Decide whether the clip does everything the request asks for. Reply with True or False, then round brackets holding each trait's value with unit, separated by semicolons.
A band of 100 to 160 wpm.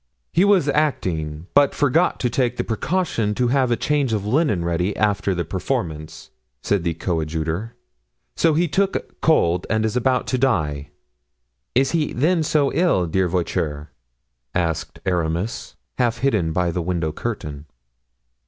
True (150 wpm)